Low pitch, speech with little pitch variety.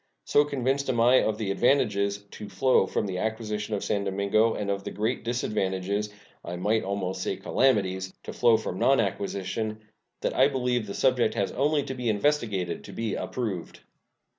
No: low, 110 Hz; average, 3.8 semitones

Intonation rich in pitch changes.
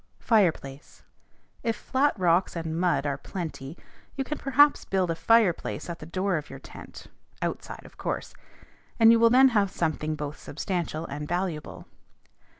Yes: wide, 6.4 semitones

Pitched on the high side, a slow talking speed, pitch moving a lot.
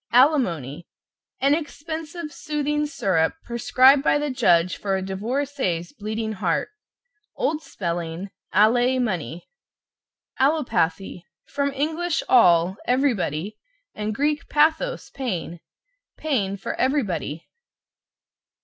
Yes: high, 240 Hz; slow, 95 wpm; wide, 8.0 semitones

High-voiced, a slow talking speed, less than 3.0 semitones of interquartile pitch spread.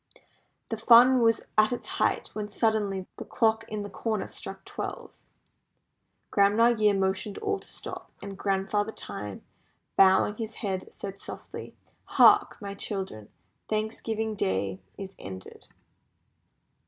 Yes: high, 205 Hz; slow, 130 wpm; narrow, 2.5 semitones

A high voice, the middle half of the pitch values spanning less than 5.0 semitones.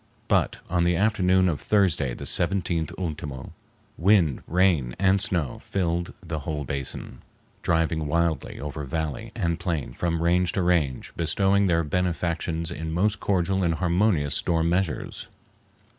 No: very low, 85 Hz; narrow, 2.6 semitones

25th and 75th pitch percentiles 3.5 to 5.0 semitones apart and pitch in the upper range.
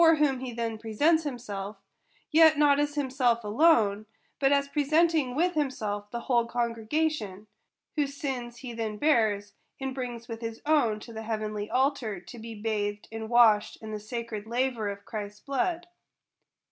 Yes: average, 4.7 semitones; high, 235 Hz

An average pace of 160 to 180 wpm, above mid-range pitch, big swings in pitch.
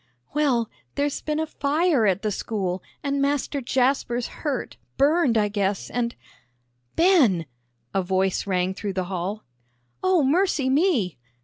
No: average, 140 wpm; high, 240 Hz; wide, 7.3 semitones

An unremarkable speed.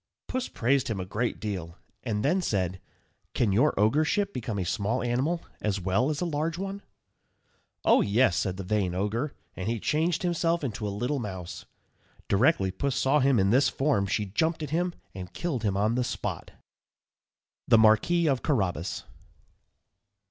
Yes: average, 170 wpm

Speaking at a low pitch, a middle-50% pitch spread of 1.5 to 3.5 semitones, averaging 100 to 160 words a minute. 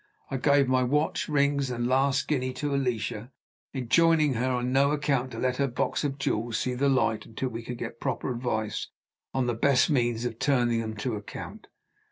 No: low, 130 Hz; average, 2.7 semitones; average, 195 wpm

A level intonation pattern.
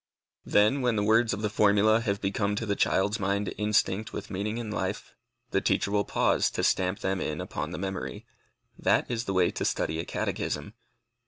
Yes: narrow, 1.9 semitones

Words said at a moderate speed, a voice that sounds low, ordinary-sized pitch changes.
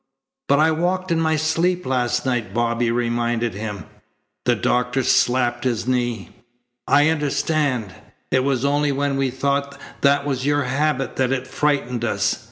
Yes: average, 155 wpm; low, 130 Hz; average, 3.1 semitones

